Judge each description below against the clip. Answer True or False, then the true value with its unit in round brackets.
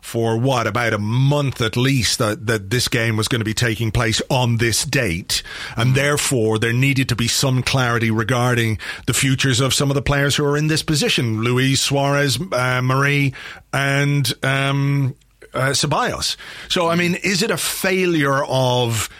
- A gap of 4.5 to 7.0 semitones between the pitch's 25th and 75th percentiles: False (3.2 semitones)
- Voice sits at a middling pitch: False (130 Hz)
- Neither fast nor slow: True (180 wpm)